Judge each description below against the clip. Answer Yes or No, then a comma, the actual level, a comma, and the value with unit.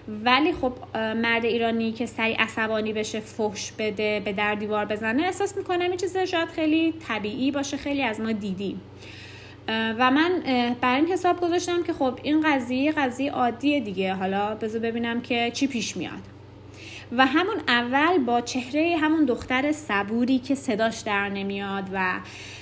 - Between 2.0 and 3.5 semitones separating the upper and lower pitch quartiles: No, average, 5.2 semitones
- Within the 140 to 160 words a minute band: Yes, fast, 155 wpm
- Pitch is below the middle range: No, high, 235 Hz